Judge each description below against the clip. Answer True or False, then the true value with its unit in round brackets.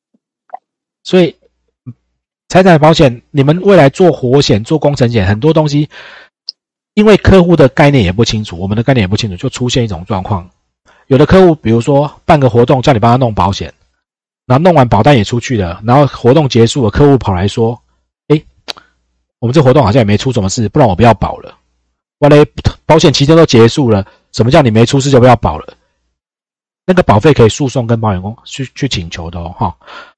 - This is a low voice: True (125 Hz)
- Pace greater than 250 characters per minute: True (300 characters per minute)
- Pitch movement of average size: False (5.9 semitones)